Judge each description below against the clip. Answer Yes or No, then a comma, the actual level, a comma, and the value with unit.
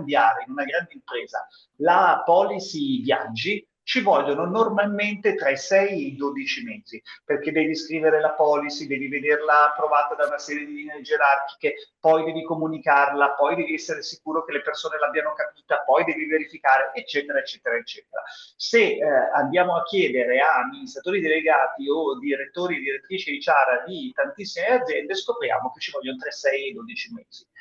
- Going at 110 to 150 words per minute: No, average, 165 wpm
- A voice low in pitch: No, medium, 165 Hz